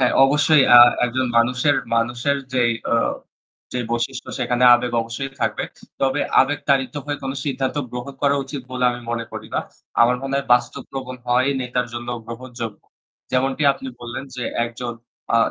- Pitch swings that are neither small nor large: No, narrow, 2.0 semitones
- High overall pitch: No, low, 125 Hz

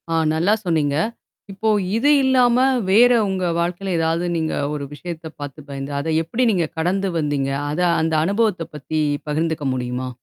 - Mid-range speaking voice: Yes, medium, 165 Hz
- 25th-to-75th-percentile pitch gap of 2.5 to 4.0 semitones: No, average, 4.7 semitones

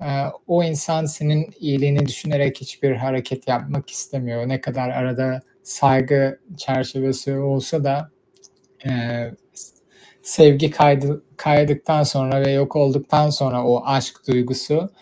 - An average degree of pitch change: No, narrow, 2.0 semitones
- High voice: No, low, 135 Hz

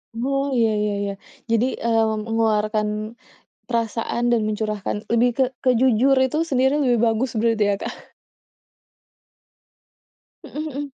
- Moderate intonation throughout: Yes, average, 3.4 semitones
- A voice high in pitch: Yes, high, 230 Hz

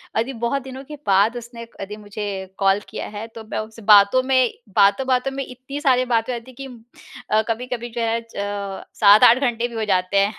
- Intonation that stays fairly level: No, average, 3.6 semitones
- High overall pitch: Yes, high, 230 Hz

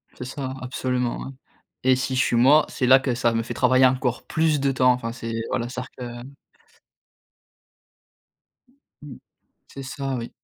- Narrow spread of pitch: Yes, narrow, 1.4 semitones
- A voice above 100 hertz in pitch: Yes, low, 130 Hz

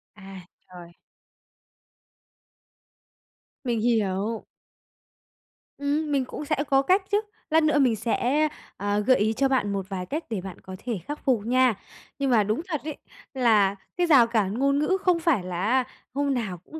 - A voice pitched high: Yes, high, 245 Hz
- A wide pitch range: Yes, wide, 5.9 semitones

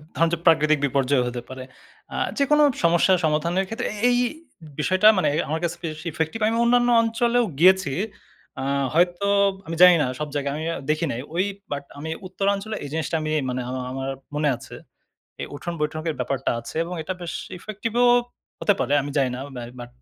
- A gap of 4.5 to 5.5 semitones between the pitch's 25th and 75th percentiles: Yes, average, 5.0 semitones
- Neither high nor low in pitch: Yes, medium, 160 Hz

